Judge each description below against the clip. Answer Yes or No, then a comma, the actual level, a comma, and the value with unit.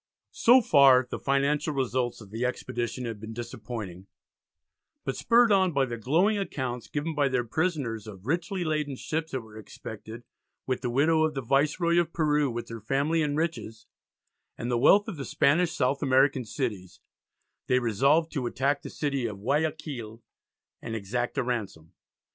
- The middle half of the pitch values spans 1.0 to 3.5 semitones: No, average, 4.8 semitones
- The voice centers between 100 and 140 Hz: Yes, low, 135 Hz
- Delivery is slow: No, average, 170 wpm